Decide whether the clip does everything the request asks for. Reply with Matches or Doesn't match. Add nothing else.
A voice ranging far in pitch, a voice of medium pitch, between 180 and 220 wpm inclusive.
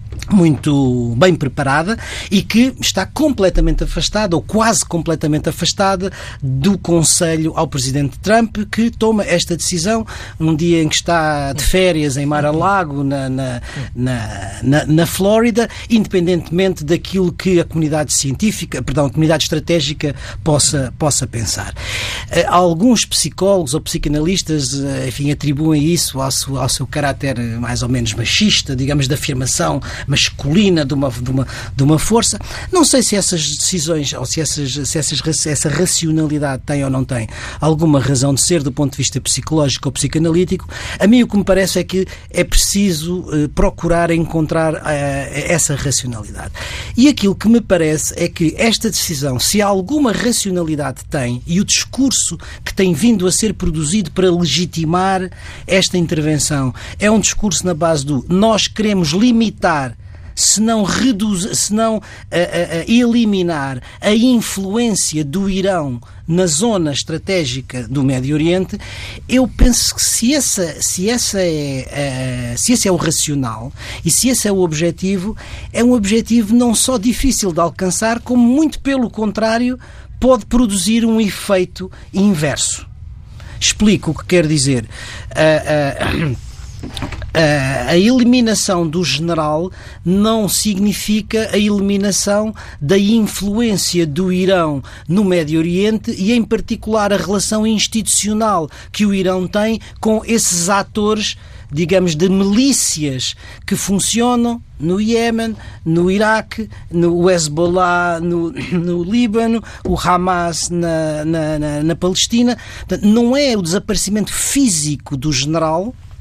Doesn't match